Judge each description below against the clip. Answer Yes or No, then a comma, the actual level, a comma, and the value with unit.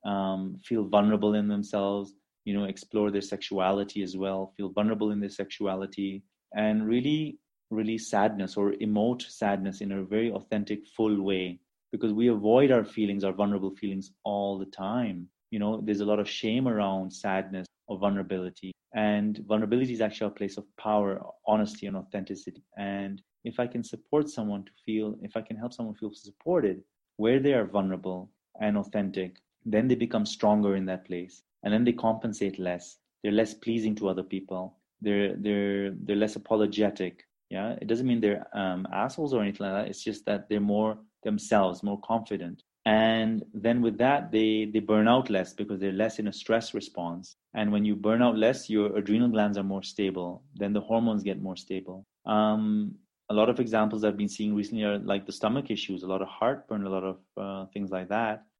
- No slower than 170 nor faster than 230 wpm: Yes, average, 190 wpm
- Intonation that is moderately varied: No, narrow, 1.9 semitones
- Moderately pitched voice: No, low, 105 Hz